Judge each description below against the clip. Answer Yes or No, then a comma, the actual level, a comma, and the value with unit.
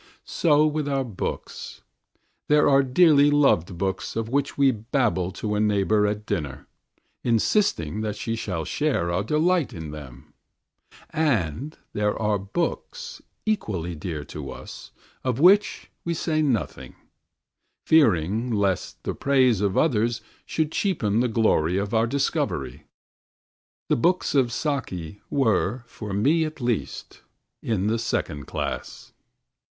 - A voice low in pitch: Yes, low, 115 Hz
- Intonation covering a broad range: Yes, wide, 6.7 semitones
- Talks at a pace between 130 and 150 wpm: Yes, slow, 135 wpm